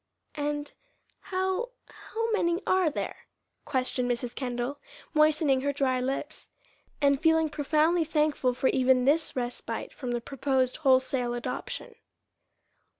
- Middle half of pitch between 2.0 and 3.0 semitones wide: No, average, 3.7 semitones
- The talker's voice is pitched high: Yes, very high, 280 Hz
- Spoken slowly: Yes, slow, 120 wpm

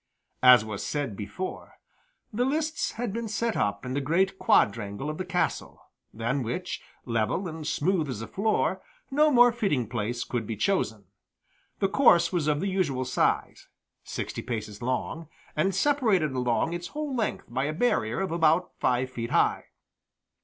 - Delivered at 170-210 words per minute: No, average, 160 wpm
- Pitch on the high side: No, medium, 155 Hz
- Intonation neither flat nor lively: No, wide, 8.3 semitones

